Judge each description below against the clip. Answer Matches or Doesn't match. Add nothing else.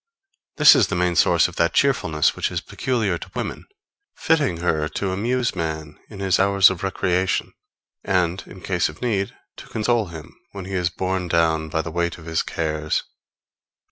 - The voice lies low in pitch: Matches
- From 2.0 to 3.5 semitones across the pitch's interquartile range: Matches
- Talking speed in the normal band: Matches